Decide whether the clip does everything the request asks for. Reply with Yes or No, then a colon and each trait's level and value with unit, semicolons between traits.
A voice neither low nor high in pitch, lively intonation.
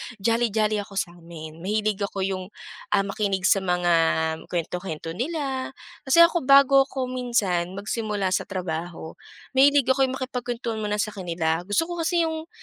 No: high, 210 Hz; wide, 6.2 semitones